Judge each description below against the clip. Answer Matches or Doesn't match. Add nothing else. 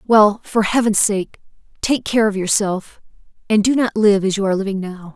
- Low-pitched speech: Doesn't match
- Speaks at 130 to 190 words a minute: Doesn't match